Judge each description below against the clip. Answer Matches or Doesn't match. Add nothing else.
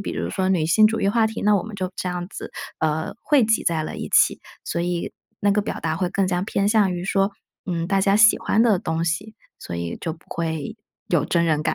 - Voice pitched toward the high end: Doesn't match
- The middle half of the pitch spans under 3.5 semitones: Doesn't match